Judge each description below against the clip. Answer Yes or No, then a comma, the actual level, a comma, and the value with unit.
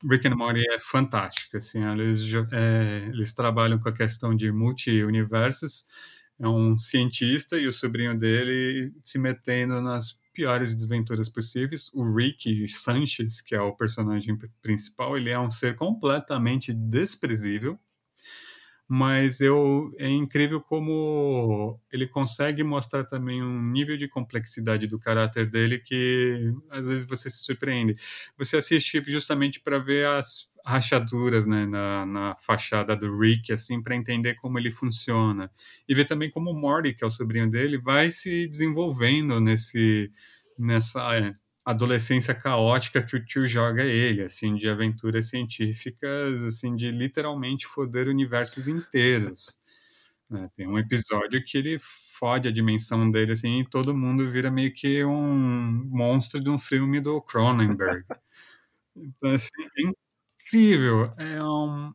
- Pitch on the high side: No, low, 125 Hz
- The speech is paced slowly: No, average, 140 wpm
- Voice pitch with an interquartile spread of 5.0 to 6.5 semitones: No, average, 3.6 semitones